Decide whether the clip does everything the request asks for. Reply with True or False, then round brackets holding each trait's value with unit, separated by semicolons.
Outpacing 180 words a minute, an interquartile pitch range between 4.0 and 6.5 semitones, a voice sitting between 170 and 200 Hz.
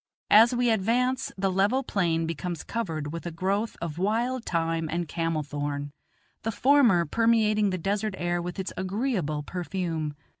False (155 wpm; 5.1 semitones; 185 Hz)